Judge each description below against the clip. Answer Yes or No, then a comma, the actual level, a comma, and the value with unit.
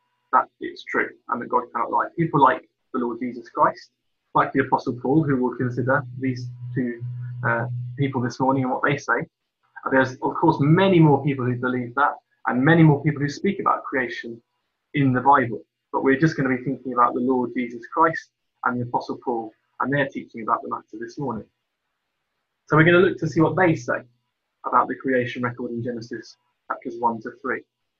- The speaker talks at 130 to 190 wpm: No, fast, 205 wpm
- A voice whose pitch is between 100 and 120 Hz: No, low, 130 Hz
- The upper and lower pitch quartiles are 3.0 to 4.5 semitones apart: Yes, average, 4.1 semitones